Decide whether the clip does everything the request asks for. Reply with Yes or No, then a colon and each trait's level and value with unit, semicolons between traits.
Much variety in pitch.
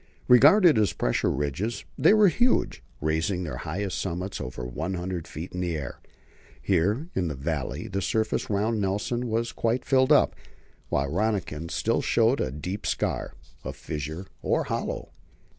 Yes: wide, 6.4 semitones